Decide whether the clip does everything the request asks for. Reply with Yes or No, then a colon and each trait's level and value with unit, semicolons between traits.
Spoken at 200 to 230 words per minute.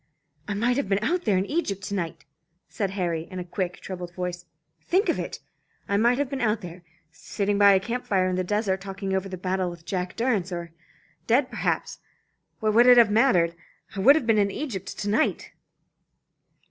Yes: fast, 205 wpm